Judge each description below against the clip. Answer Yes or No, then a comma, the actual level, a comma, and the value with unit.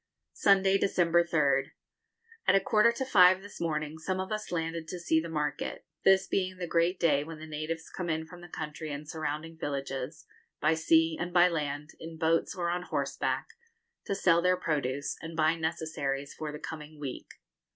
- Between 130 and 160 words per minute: No, average, 185 wpm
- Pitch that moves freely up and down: No, average, 2.8 semitones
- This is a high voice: No, medium, 160 Hz